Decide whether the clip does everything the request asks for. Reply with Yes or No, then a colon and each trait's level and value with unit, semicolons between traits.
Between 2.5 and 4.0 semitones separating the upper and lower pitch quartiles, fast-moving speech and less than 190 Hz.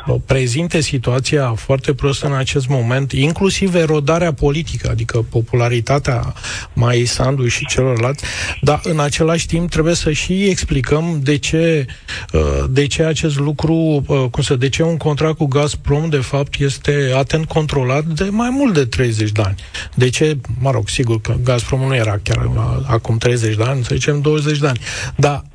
No: average, 3.7 semitones; average, 160 wpm; medium, 140 Hz